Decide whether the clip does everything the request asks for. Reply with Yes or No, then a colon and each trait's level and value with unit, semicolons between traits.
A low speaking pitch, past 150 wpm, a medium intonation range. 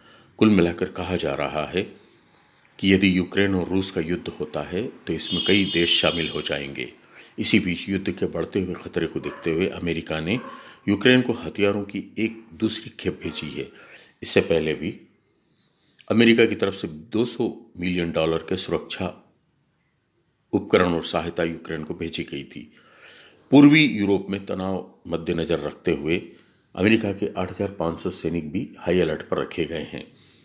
Yes: very low, 95 Hz; average, 160 wpm; average, 3.6 semitones